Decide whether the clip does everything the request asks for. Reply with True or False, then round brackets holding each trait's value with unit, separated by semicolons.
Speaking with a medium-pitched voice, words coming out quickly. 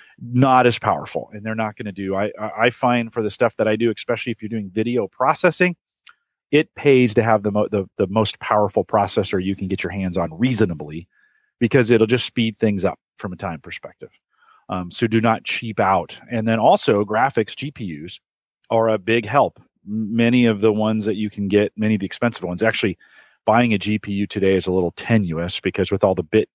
False (110 Hz; 210 wpm)